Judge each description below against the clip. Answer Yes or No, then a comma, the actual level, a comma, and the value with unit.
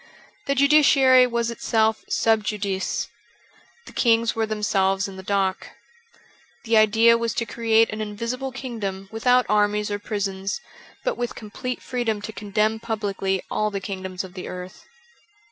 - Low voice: No, high, 215 Hz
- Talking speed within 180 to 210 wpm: No, average, 145 wpm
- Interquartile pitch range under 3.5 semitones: Yes, average, 2.8 semitones